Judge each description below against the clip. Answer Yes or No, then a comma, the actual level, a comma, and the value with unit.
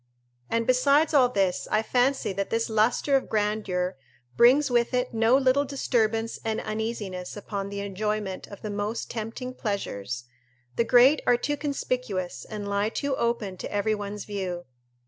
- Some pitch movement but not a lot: Yes, average, 3.7 semitones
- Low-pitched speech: No, high, 220 Hz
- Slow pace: No, average, 160 wpm